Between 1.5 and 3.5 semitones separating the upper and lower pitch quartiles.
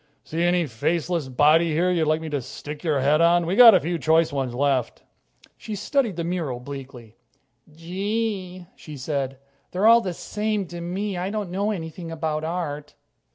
No: average, 3.9 semitones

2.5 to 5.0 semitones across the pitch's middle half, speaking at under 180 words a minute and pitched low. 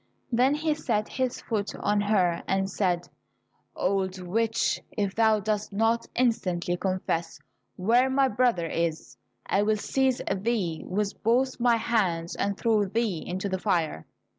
No: average, 4.0 semitones; average, 145 wpm; high, 205 Hz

